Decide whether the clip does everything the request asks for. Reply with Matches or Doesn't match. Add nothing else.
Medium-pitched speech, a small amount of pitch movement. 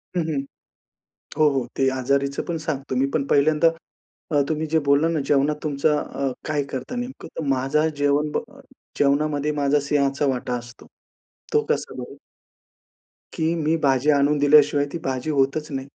Matches